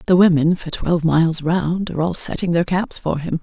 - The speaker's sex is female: Yes, female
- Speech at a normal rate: No, fast, 230 wpm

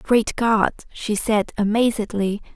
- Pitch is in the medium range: No, high, 215 Hz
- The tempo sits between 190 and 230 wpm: No, slow, 115 wpm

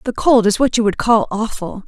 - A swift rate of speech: Yes, fast, 255 wpm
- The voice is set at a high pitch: Yes, high, 220 Hz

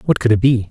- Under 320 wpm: No, fast, 340 wpm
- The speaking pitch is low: Yes, low, 115 Hz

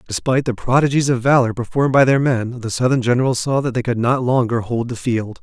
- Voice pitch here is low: Yes, low, 125 Hz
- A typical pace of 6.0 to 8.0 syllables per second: Yes, 6.1 syllables/s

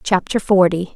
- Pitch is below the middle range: No, medium, 185 Hz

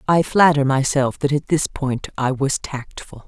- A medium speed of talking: Yes, average, 185 wpm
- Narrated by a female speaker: Yes, female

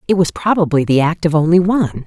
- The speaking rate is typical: No, fast, 235 wpm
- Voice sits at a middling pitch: Yes, medium, 165 Hz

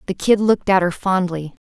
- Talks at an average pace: No, fast, 215 wpm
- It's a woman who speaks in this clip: Yes, female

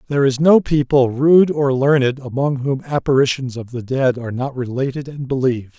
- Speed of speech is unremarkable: Yes, average, 185 wpm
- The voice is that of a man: Yes, male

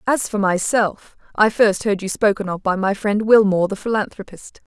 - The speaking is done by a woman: Yes, female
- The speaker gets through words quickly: No, average, 190 wpm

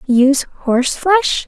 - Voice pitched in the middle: No, very high, 285 Hz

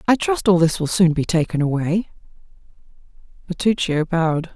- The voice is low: No, medium, 175 Hz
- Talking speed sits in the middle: Yes, average, 145 wpm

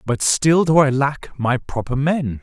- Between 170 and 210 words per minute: Yes, average, 200 wpm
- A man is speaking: Yes, male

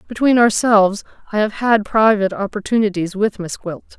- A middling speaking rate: Yes, average, 150 wpm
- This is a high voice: Yes, high, 210 Hz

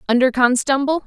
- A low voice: No, very high, 265 Hz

